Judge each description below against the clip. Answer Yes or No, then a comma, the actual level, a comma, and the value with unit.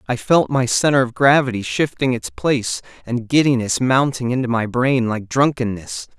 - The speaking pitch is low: Yes, low, 125 Hz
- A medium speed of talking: Yes, average, 165 wpm